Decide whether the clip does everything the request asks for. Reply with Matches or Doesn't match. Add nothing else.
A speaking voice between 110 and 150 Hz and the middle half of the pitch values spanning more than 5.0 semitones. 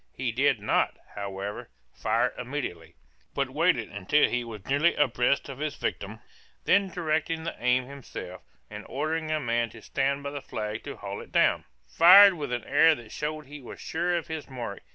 Matches